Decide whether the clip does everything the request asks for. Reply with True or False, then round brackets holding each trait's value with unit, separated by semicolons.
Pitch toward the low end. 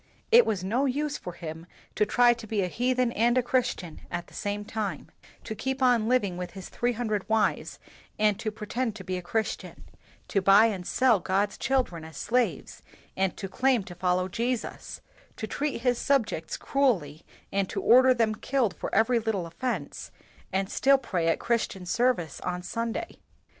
False (220 Hz)